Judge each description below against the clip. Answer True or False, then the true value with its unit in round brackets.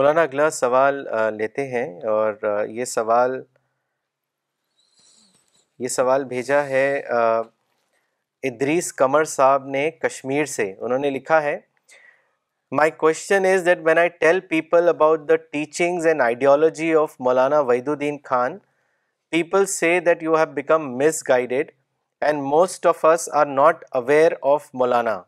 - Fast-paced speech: False (135 wpm)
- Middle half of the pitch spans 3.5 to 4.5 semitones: True (3.8 semitones)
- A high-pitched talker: False (145 Hz)